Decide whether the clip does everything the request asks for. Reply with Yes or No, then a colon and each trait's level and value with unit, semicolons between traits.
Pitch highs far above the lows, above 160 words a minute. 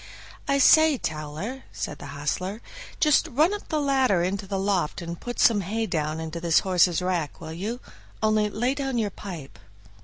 Yes: wide, 6.8 semitones; average, 180 wpm